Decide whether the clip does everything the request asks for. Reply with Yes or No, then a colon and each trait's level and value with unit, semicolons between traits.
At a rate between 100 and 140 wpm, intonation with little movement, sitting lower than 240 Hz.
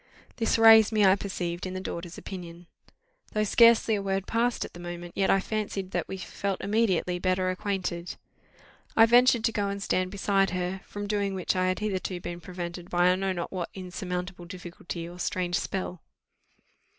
No: average, 185 wpm; narrow, 2.2 semitones; medium, 185 Hz